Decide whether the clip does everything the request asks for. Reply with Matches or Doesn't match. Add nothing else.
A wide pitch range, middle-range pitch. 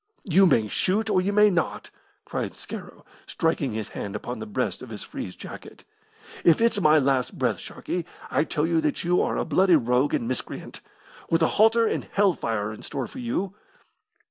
Matches